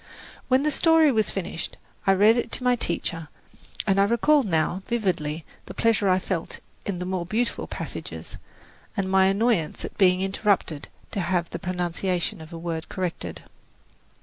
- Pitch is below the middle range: No, high, 190 Hz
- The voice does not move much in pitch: No, average, 4.4 semitones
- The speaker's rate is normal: Yes, average, 165 wpm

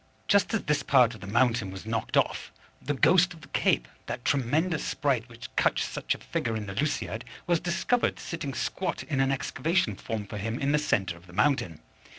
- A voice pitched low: Yes, low, 130 Hz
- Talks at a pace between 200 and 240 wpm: Yes, fast, 205 wpm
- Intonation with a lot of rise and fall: Yes, wide, 6.2 semitones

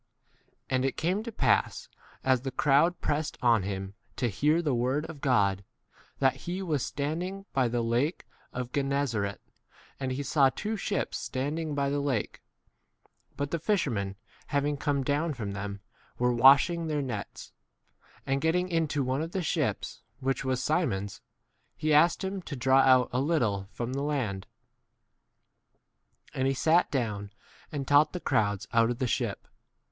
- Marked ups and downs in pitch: No, average, 4.3 semitones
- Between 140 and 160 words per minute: No, average, 175 wpm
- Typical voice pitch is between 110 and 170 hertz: Yes, low, 135 Hz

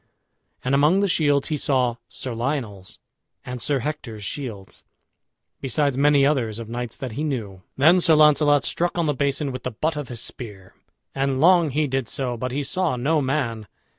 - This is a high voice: No, low, 135 Hz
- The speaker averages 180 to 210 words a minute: Yes, average, 185 wpm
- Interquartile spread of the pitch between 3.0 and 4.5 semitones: Yes, average, 3.8 semitones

